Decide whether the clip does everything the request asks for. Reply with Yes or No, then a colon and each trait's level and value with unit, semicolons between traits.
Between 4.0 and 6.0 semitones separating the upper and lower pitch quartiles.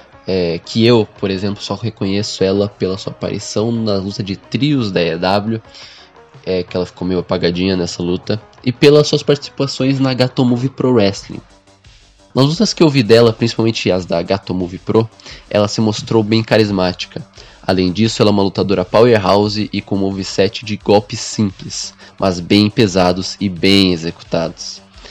No: average, 3.3 semitones